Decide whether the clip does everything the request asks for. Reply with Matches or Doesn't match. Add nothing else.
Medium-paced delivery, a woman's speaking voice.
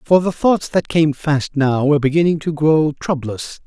Doesn't match